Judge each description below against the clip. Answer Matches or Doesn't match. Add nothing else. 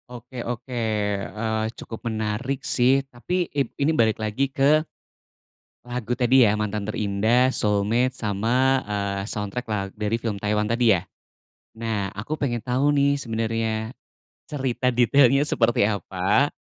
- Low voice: Matches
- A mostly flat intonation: Doesn't match